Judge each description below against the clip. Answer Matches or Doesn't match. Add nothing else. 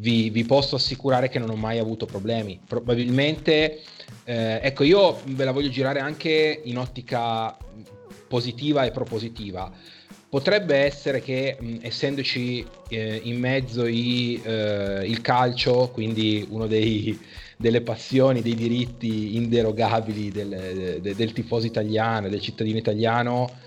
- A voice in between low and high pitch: Doesn't match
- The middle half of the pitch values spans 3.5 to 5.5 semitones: Doesn't match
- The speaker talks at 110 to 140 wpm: Matches